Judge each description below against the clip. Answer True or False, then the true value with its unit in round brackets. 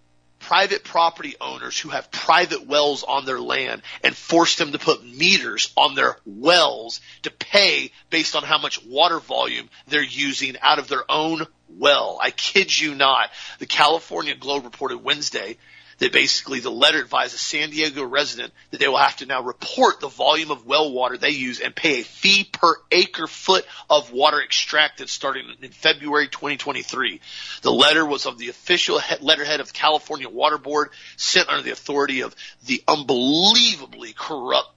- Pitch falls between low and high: True (150 Hz)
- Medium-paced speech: True (175 wpm)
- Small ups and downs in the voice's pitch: True (2.2 semitones)